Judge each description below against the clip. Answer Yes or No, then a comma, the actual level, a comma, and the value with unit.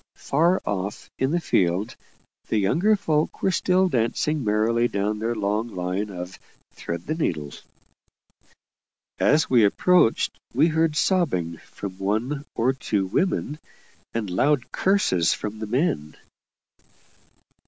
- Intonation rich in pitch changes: Yes, wide, 7.6 semitones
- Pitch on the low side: Yes, low, 115 Hz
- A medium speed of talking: No, slow, 125 wpm